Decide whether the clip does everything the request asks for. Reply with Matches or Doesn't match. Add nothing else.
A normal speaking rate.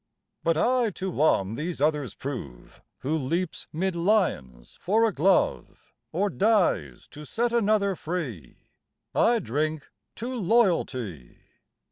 Doesn't match